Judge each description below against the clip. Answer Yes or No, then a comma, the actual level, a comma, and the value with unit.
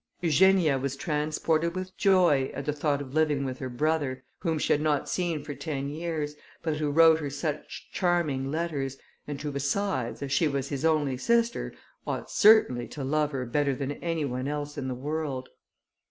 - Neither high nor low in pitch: Yes, medium, 150 Hz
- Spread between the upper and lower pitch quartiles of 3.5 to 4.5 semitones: No, average, 2.8 semitones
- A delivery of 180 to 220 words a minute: Yes, average, 185 wpm